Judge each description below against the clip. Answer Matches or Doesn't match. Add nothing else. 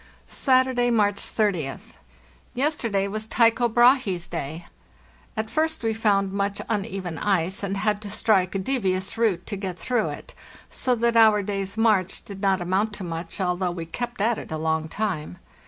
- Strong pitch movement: Doesn't match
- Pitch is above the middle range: Matches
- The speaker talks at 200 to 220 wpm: Doesn't match